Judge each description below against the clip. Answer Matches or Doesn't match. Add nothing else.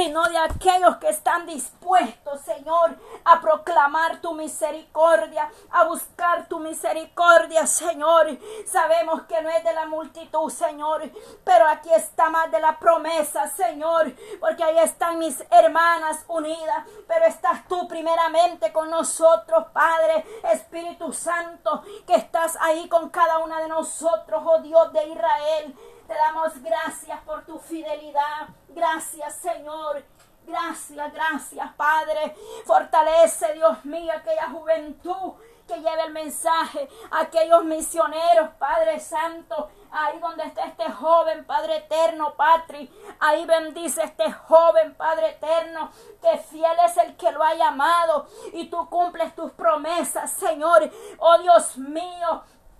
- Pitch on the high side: Matches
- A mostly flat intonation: Matches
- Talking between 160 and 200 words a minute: Doesn't match